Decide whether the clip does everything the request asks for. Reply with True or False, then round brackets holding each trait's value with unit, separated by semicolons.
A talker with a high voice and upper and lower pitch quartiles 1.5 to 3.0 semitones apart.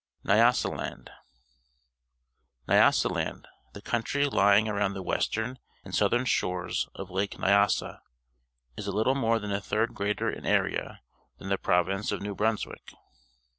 False (105 Hz; 2.4 semitones)